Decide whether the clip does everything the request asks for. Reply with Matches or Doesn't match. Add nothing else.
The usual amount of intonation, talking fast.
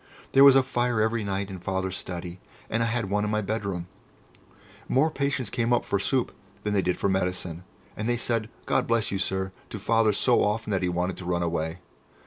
Matches